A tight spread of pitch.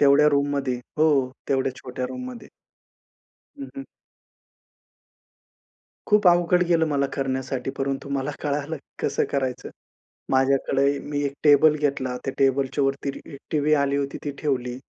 Yes: narrow, 2.0 semitones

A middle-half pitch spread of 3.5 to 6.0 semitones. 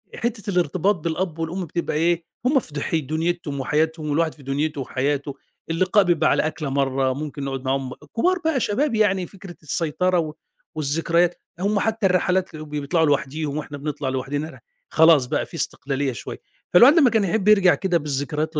Yes: average, 4.3 semitones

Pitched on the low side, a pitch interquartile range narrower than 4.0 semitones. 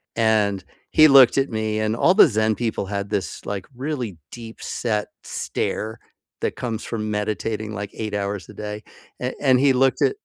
Yes: low, 110 Hz; average, 3.0 semitones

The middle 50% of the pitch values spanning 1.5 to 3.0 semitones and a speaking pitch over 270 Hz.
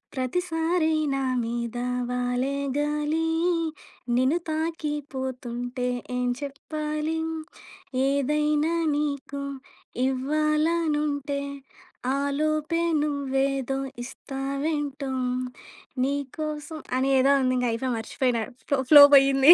Yes: average, 2.7 semitones; very high, 280 Hz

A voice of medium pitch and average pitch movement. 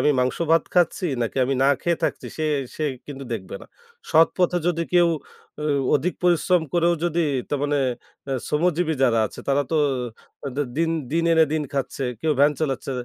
Yes: medium, 155 Hz; average, 3.4 semitones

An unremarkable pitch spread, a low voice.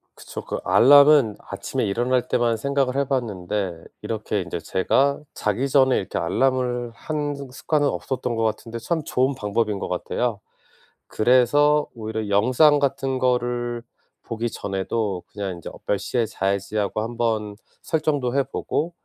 Yes: average, 4.4 semitones; low, 120 Hz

